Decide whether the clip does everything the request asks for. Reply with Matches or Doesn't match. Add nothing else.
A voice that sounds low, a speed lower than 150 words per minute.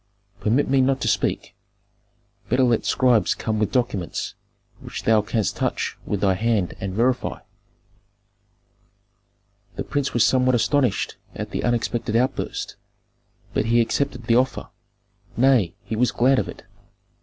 Matches